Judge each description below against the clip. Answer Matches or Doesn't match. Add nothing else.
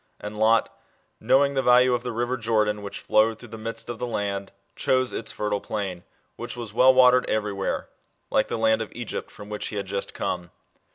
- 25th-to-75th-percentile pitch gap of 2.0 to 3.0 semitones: Matches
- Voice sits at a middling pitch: Doesn't match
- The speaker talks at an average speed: Doesn't match